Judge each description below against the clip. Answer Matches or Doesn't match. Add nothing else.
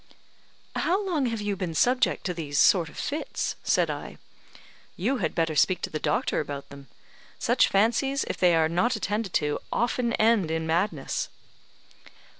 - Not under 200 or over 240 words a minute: Doesn't match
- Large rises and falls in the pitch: Matches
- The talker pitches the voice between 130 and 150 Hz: Doesn't match